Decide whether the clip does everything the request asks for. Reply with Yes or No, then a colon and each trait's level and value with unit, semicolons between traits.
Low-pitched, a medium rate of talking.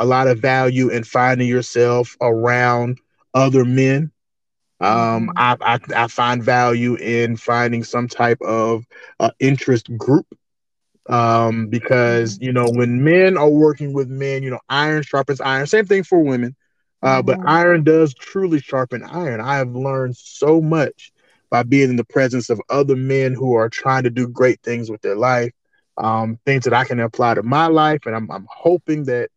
Yes: low, 125 Hz; average, 180 wpm